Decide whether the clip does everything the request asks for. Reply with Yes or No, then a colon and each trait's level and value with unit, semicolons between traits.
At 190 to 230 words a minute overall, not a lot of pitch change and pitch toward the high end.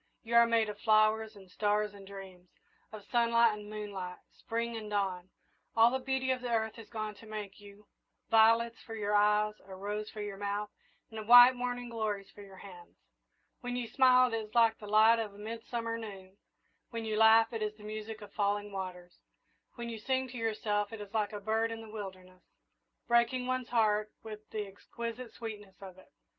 Yes: average, 200 wpm; narrow, 2.0 semitones; high, 215 Hz